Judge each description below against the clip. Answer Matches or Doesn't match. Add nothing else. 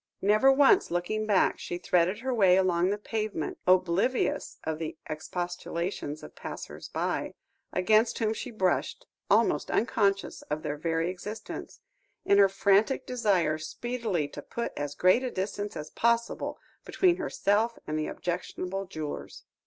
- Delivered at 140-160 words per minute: Matches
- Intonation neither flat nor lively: Matches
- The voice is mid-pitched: Doesn't match